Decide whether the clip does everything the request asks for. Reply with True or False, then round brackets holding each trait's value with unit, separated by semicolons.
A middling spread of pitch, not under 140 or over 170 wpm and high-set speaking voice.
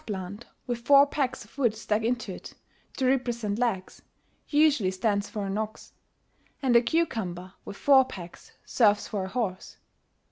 True (4.1 semitones; 165 wpm; 225 Hz)